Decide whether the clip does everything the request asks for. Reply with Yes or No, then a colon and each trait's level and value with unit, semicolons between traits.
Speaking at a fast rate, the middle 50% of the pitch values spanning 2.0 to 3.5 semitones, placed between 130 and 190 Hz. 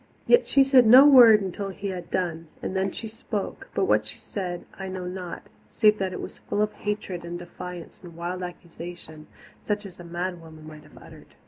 Yes: fast, 210 wpm; average, 3.2 semitones; medium, 185 Hz